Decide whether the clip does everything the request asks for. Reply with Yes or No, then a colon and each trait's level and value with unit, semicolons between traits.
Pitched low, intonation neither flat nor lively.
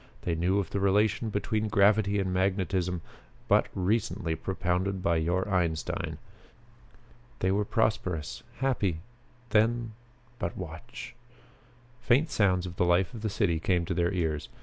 Yes: very low, 95 Hz; average, 3.1 semitones